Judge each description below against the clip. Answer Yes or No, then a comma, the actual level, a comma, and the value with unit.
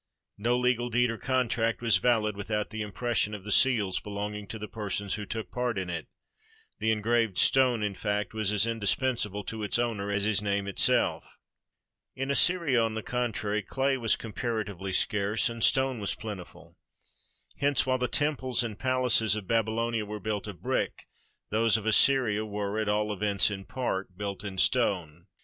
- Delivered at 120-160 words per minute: No, average, 175 wpm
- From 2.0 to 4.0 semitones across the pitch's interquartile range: Yes, average, 2.8 semitones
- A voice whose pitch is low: Yes, low, 110 Hz